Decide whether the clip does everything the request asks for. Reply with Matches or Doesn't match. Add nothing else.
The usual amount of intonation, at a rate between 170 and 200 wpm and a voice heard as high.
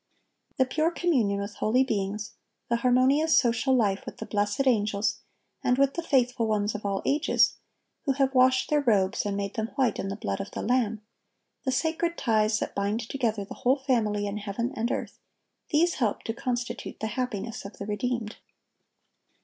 Matches